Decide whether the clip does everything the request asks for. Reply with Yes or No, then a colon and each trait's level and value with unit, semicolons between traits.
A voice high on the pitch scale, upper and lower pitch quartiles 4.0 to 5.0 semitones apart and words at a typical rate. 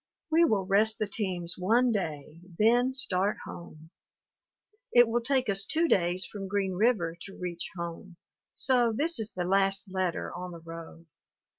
Yes: high, 195 Hz; average, 4.5 semitones; average, 160 wpm